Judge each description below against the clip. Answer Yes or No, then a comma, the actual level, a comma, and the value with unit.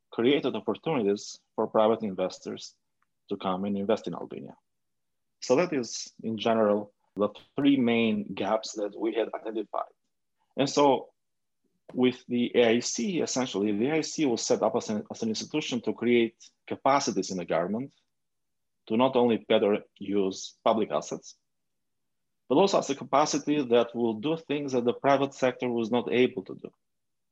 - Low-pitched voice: Yes, low, 120 Hz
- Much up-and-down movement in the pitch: No, average, 3.9 semitones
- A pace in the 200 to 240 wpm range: No, average, 155 wpm